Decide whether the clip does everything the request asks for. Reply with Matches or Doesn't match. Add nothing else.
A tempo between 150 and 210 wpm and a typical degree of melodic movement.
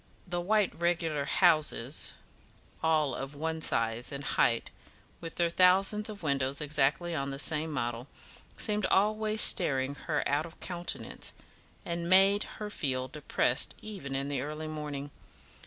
Doesn't match